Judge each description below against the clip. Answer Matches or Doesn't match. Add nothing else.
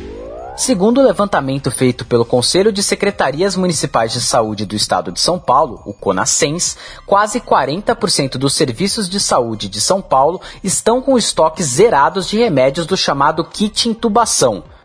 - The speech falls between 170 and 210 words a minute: Doesn't match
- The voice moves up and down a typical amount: Doesn't match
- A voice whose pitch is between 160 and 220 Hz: Matches